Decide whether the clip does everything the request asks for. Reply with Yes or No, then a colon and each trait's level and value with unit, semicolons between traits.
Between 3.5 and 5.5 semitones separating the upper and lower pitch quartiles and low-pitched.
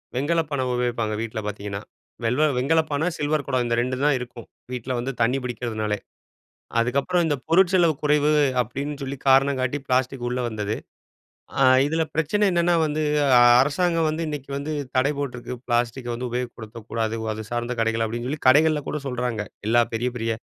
Yes: average, 3.9 semitones; low, 130 Hz